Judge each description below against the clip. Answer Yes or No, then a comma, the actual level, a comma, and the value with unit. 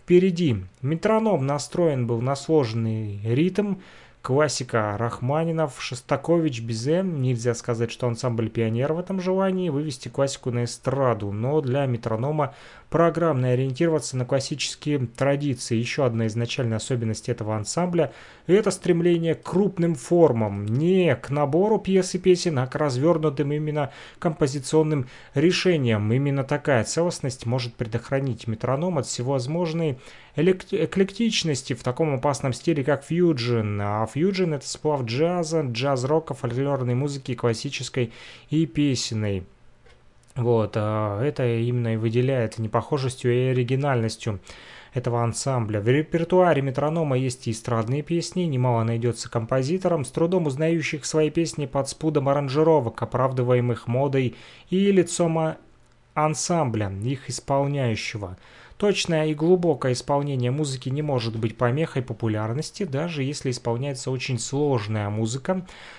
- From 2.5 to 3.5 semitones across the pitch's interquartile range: No, average, 4.9 semitones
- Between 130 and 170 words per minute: No, average, 120 wpm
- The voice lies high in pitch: No, medium, 140 Hz